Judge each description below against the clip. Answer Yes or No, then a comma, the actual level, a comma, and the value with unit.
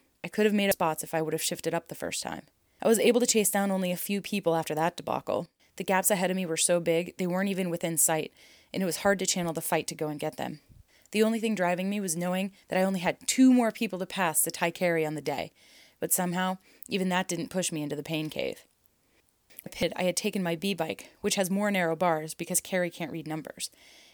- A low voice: No, medium, 180 Hz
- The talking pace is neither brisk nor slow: No, fast, 255 wpm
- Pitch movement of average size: Yes, average, 3.1 semitones